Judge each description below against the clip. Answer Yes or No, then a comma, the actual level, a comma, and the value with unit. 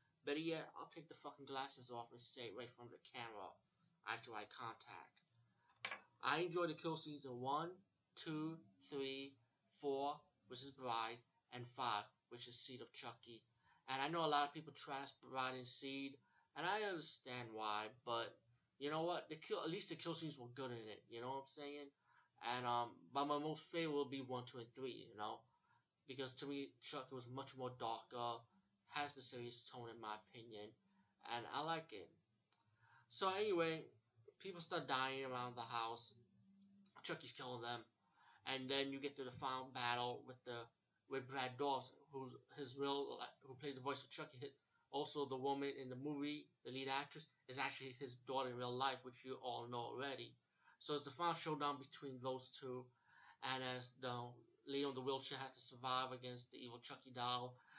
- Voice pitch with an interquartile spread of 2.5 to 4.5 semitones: Yes, average, 2.9 semitones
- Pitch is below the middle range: Yes, low, 130 Hz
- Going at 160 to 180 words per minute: No, average, 190 wpm